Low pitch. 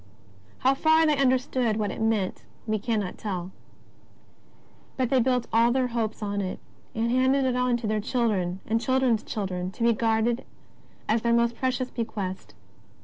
No: high, 230 Hz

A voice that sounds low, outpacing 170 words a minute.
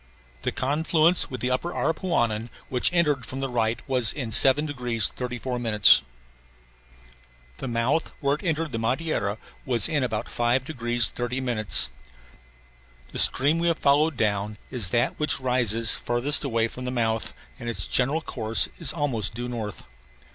No: low, 125 Hz; average, 160 wpm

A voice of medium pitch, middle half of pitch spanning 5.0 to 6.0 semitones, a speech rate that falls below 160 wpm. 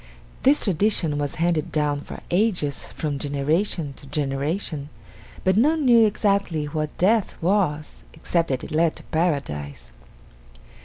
Yes: medium, 160 Hz; average, 5.3 semitones; slow, 135 wpm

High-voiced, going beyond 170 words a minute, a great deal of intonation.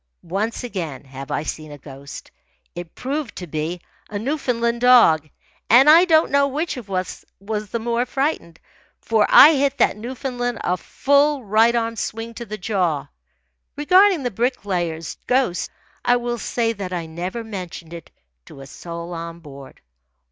No: high, 220 Hz; average, 160 wpm; wide, 6.7 semitones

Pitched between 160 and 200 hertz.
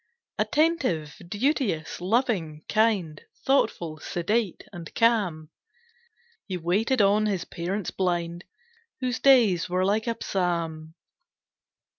Yes: high, 190 Hz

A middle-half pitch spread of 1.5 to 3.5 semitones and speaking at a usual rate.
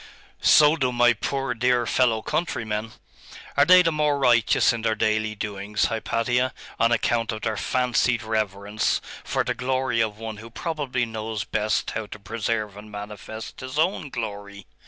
Yes: average, 2.9 semitones; average, 160 wpm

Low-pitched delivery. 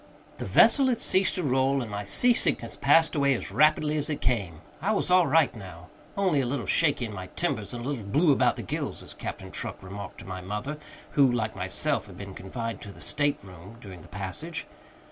Yes: low, 120 Hz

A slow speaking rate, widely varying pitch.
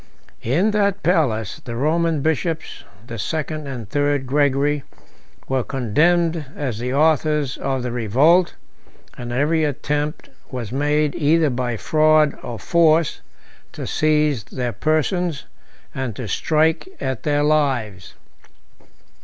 No: slow, 120 wpm; average, 3.8 semitones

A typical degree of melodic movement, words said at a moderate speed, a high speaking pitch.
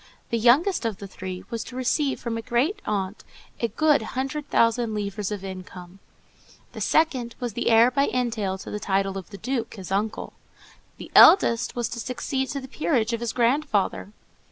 Yes: average, 4.2 semitones; average, 180 wpm; high, 230 Hz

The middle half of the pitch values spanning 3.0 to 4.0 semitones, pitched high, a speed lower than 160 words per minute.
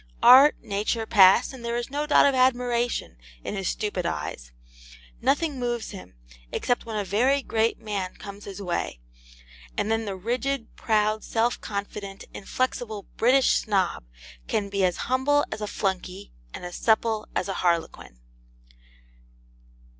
Yes: average, 3.7 semitones; high, 220 Hz; average, 145 wpm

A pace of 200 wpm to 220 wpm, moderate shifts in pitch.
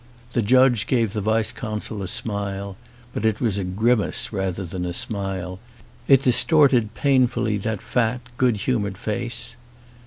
No: average, 150 wpm; average, 3.5 semitones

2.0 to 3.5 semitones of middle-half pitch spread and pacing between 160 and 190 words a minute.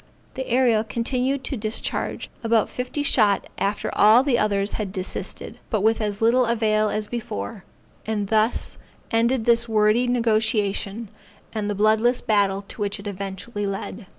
No: narrow, 2.4 semitones; average, 150 wpm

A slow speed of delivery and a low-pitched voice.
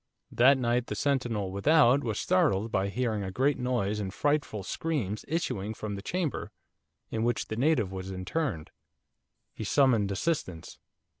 No: average, 150 wpm; low, 115 Hz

